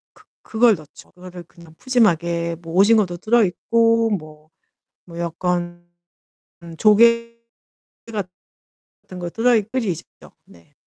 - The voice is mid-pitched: Yes, medium, 180 Hz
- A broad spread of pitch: No, average, 5.0 semitones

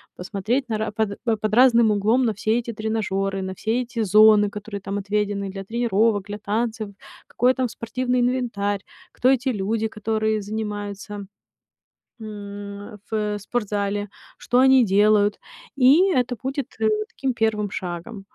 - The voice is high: Yes, high, 215 Hz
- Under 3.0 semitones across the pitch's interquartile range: Yes, narrow, 2.6 semitones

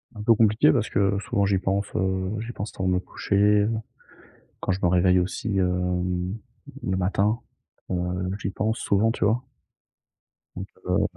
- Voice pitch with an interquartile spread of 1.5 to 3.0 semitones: Yes, narrow, 2.4 semitones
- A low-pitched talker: Yes, very low, 95 Hz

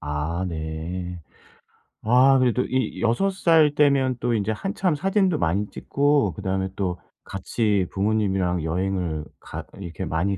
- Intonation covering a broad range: Yes, wide, 6.8 semitones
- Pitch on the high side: No, low, 100 Hz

